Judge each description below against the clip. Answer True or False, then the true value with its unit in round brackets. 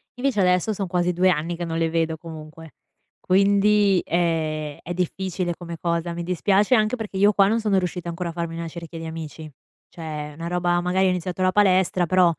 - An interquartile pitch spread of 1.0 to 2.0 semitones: False (2.4 semitones)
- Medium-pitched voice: True (175 Hz)